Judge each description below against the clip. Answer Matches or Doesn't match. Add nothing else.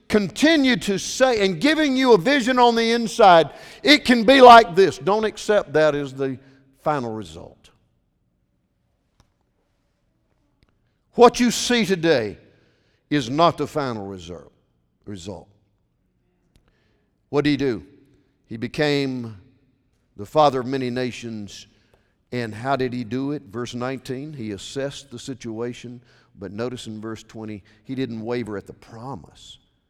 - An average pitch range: Doesn't match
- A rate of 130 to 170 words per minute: Matches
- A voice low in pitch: Matches